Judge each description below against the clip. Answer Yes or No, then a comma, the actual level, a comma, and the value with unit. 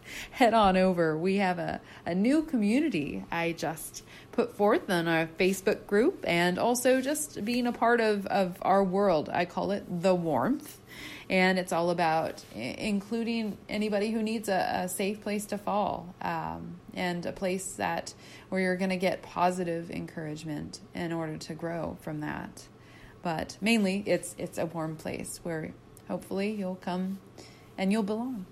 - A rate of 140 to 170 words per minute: Yes, average, 165 wpm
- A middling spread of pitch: Yes, average, 3.6 semitones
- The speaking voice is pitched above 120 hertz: Yes, high, 190 Hz